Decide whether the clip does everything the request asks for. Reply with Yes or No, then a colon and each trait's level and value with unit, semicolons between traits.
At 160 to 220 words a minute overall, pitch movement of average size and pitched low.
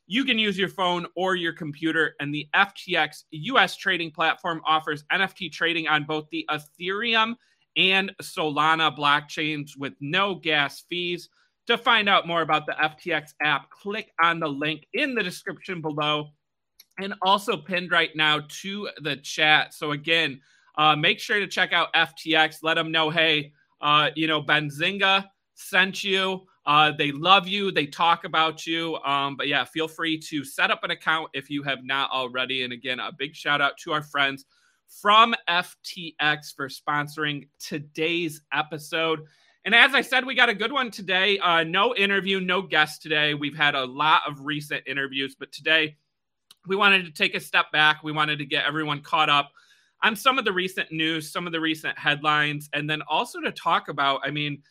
No: average, 185 wpm; average, 3.6 semitones; medium, 160 Hz